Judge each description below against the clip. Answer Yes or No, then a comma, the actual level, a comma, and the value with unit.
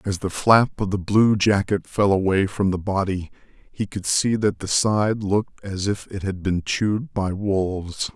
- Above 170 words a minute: Yes, average, 200 wpm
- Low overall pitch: Yes, low, 100 Hz